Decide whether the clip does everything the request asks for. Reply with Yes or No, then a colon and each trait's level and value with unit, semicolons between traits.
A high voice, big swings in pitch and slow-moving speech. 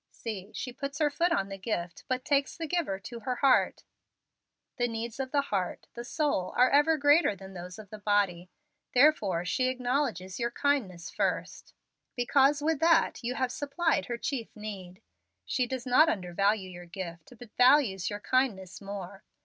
No: high, 235 Hz; wide, 6.3 semitones; average, 175 wpm